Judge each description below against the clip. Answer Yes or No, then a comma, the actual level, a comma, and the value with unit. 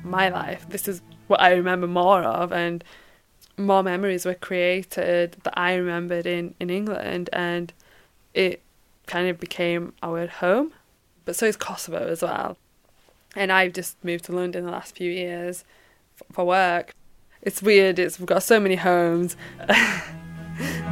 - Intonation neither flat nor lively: No, narrow, 1.4 semitones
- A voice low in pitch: No, medium, 180 Hz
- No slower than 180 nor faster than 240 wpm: No, average, 155 wpm